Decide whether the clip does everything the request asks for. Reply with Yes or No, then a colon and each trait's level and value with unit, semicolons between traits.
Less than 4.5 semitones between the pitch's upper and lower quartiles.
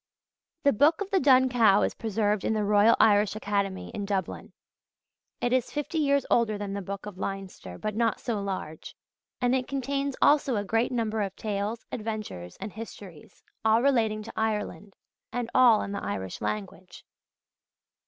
Yes: average, 3.5 semitones